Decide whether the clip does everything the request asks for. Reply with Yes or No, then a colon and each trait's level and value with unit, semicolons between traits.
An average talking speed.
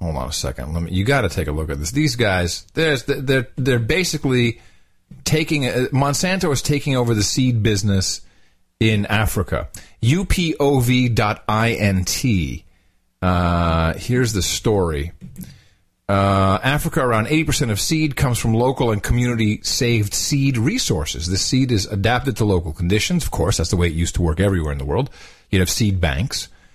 Yes: average, 175 wpm